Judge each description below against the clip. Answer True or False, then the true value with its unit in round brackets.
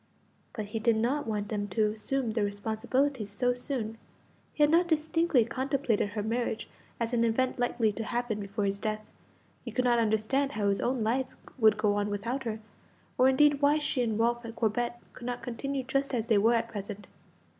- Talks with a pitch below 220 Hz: False (230 Hz)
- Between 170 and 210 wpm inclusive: True (195 wpm)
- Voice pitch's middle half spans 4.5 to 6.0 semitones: False (3.3 semitones)